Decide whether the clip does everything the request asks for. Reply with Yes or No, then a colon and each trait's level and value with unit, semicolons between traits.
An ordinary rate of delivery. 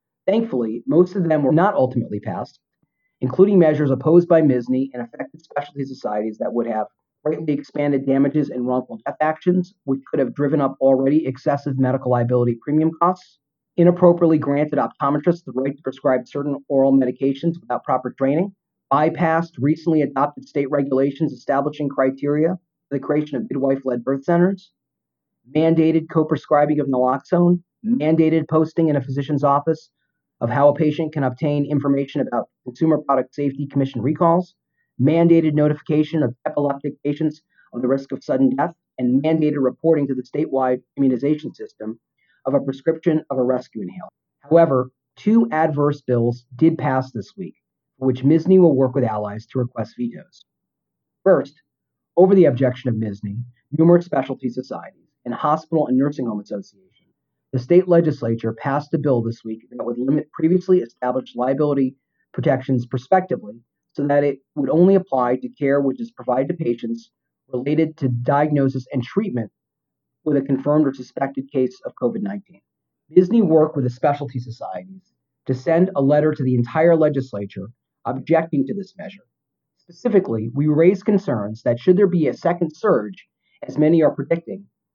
Yes: average, 160 wpm